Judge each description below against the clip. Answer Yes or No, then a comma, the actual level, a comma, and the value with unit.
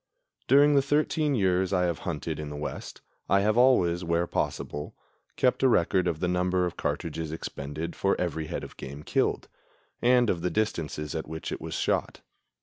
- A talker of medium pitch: No, very low, 90 Hz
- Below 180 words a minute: No, average, 185 wpm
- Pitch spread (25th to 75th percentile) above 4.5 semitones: Yes, average, 5.1 semitones